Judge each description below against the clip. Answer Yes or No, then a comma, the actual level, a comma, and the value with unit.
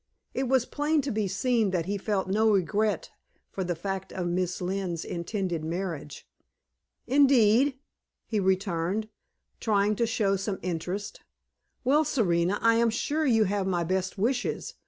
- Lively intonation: No, average, 3.8 semitones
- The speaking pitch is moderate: No, high, 200 Hz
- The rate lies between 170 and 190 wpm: No, average, 150 wpm